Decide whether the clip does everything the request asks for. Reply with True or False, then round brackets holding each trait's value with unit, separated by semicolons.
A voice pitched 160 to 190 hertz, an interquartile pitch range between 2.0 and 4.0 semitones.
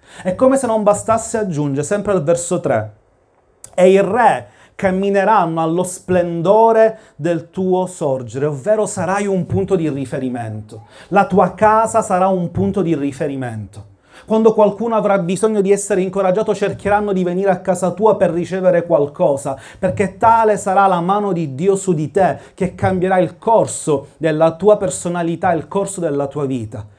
False (185 Hz; 4.6 semitones)